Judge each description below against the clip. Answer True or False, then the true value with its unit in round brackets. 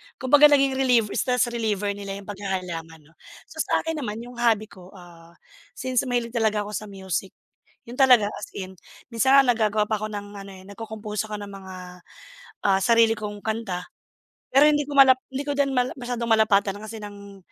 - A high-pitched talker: True (215 Hz)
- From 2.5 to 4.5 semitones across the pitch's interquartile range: True (3.7 semitones)